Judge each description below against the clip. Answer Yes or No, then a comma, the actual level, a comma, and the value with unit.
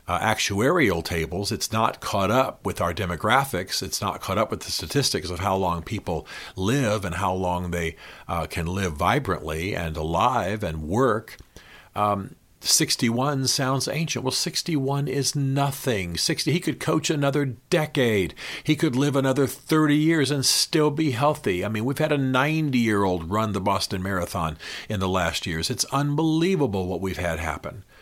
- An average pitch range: No, wide, 7.3 semitones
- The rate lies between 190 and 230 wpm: No, average, 165 wpm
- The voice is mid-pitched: No, low, 110 Hz